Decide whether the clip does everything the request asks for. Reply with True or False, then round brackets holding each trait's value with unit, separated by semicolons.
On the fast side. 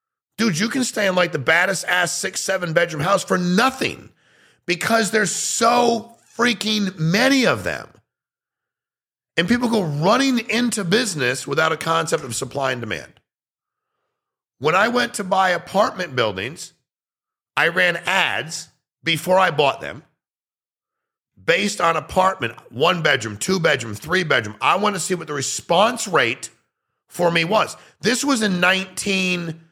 False (150 wpm)